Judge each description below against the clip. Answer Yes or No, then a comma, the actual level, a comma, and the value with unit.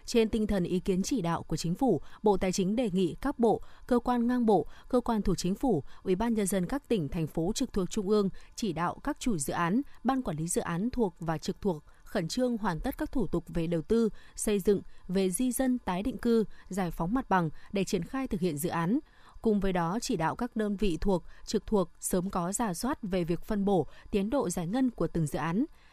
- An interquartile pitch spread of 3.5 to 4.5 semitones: No, average, 5.0 semitones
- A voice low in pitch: No, high, 200 Hz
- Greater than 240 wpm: Yes, fast, 250 wpm